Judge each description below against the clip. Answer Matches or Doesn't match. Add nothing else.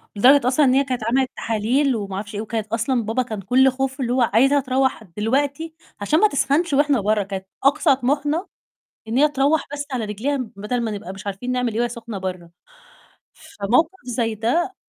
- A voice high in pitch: Matches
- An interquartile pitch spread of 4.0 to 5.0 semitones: Matches